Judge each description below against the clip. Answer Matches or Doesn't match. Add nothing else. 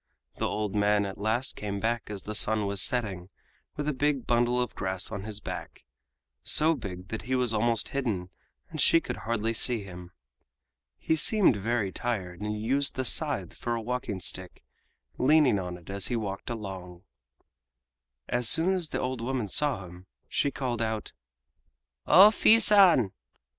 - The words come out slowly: Doesn't match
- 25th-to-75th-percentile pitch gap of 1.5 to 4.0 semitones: Doesn't match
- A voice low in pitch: Matches